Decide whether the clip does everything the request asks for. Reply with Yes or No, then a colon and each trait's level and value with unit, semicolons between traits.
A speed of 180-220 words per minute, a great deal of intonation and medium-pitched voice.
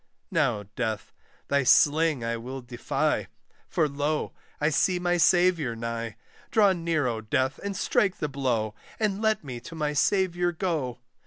No: average, 155 wpm; wide, 6.3 semitones; medium, 150 Hz